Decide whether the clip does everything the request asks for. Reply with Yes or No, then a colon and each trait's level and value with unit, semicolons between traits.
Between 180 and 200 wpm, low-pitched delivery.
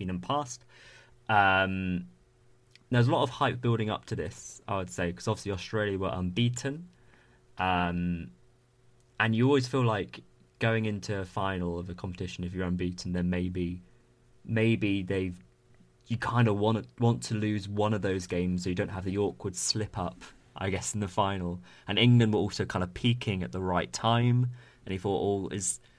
Yes: average, 185 wpm; low, 105 Hz